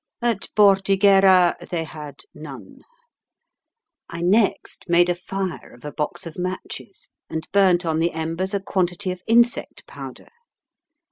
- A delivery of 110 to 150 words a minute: Yes, slow, 135 wpm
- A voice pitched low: No, medium, 180 Hz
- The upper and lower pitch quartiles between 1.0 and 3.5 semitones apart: Yes, narrow, 2.6 semitones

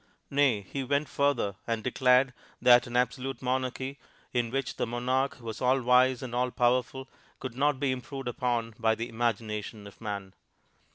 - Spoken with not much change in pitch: Yes, narrow, 2.2 semitones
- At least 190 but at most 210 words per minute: No, average, 165 wpm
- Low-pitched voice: Yes, low, 125 Hz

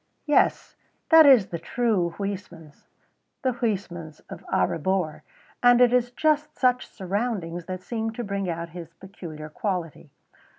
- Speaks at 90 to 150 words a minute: Yes, average, 140 wpm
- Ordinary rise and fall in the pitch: No, wide, 6.2 semitones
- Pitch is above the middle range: Yes, high, 195 Hz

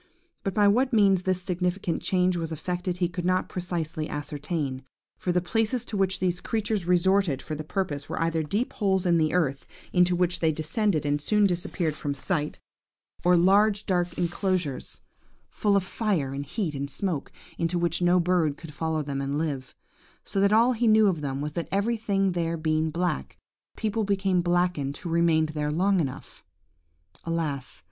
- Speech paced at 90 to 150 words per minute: No, average, 180 wpm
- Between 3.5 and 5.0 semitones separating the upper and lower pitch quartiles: Yes, average, 3.8 semitones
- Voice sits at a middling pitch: Yes, medium, 175 Hz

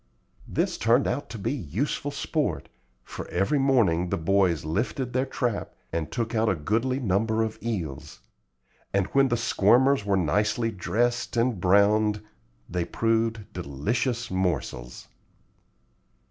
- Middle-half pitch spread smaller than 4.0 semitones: No, average, 4.7 semitones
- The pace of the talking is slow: Yes, slow, 130 wpm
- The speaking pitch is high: No, low, 110 Hz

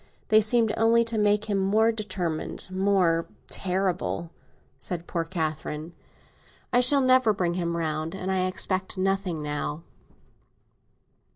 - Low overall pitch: No, high, 190 Hz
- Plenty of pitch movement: No, average, 4.1 semitones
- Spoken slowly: Yes, slow, 120 wpm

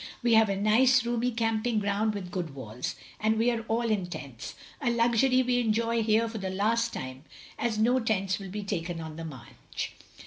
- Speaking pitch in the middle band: No, high, 220 Hz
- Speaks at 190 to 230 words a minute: Yes, average, 200 wpm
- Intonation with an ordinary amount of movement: Yes, average, 3.6 semitones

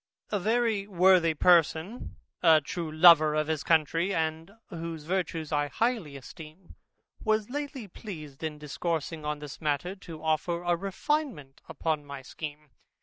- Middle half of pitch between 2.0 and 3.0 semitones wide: No, average, 3.7 semitones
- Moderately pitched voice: Yes, medium, 165 Hz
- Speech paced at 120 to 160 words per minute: Yes, average, 145 wpm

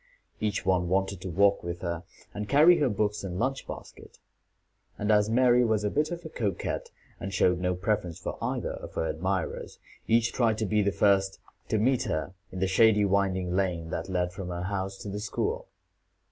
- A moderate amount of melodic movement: Yes, average, 3.1 semitones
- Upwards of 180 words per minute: Yes, average, 200 wpm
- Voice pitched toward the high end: No, low, 100 Hz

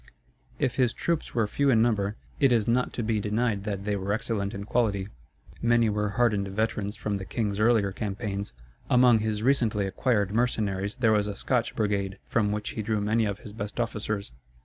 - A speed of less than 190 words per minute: No, average, 195 wpm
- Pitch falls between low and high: No, low, 105 Hz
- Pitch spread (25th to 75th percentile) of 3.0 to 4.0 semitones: No, narrow, 2.4 semitones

